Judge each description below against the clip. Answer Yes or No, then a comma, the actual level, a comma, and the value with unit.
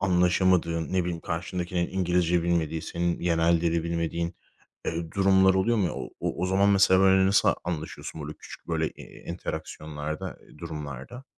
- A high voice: No, very low, 85 Hz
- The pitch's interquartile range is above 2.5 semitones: No, narrow, 2.2 semitones